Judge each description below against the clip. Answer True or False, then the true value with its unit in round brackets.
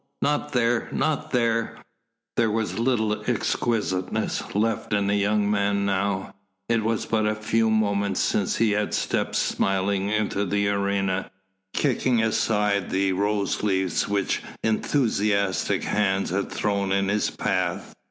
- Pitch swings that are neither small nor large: False (2.0 semitones)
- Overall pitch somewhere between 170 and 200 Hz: False (105 Hz)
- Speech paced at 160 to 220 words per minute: False (135 wpm)